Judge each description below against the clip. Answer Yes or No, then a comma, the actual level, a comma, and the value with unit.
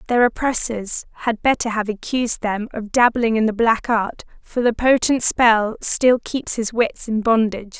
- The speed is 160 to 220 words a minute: Yes, average, 175 wpm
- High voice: Yes, high, 230 Hz